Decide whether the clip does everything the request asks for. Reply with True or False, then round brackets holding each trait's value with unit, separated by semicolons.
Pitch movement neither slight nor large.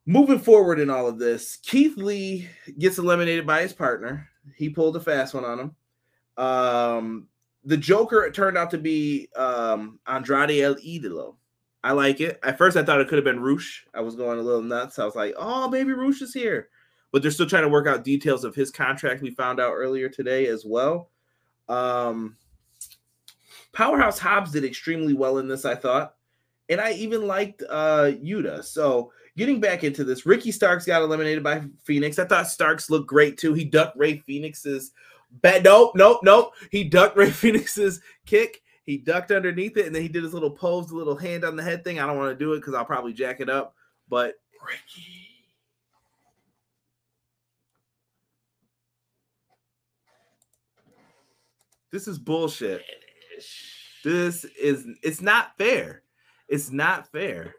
False (6.0 semitones)